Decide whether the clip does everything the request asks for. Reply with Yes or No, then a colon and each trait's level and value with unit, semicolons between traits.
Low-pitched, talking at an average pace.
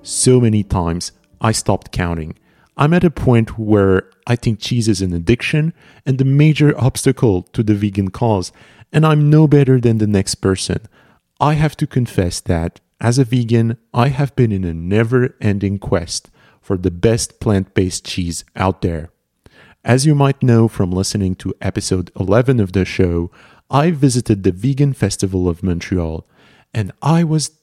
Yes: low, 110 Hz; average, 170 wpm